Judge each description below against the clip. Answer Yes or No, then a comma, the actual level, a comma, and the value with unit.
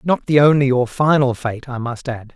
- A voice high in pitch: No, low, 130 Hz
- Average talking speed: No, fast, 230 wpm